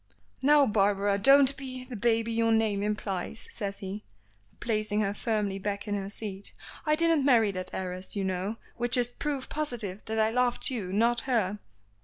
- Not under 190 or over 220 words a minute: No, average, 175 wpm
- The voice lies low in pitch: No, high, 220 Hz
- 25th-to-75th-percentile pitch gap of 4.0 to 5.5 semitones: No, average, 3.5 semitones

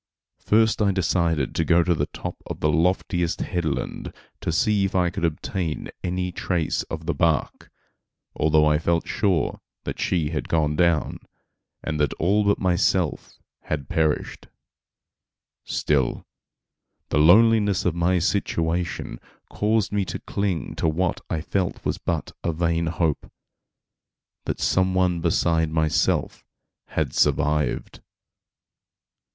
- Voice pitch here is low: Yes, very low, 85 Hz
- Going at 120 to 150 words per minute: Yes, slow, 135 wpm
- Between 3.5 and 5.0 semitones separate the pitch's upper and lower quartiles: No, average, 2.8 semitones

